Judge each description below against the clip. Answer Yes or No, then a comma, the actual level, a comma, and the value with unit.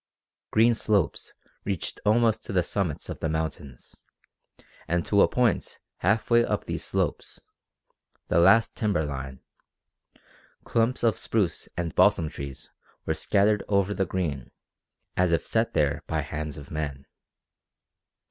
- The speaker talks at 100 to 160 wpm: Yes, average, 140 wpm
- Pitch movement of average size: No, wide, 5.8 semitones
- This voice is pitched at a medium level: No, very low, 90 Hz